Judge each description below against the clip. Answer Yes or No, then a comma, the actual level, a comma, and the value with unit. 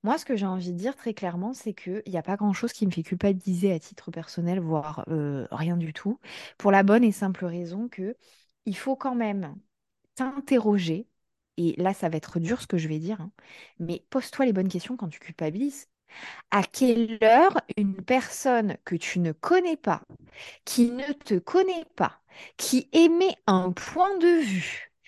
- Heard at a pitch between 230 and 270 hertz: No, high, 200 Hz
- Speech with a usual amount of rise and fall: No, wide, 6.2 semitones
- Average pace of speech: Yes, average, 190 wpm